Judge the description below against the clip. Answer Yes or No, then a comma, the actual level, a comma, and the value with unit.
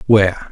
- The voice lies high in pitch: No, low, 100 Hz